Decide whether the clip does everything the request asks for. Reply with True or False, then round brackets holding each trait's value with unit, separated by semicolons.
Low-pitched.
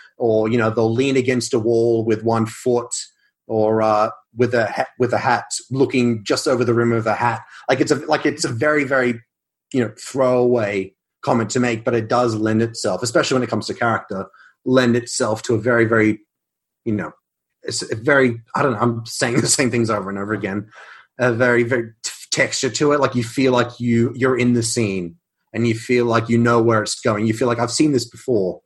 True (120 Hz)